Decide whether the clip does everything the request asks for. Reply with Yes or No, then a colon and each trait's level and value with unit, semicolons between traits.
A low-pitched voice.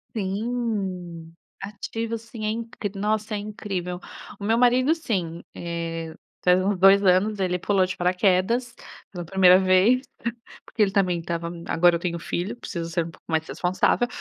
No: high, 190 Hz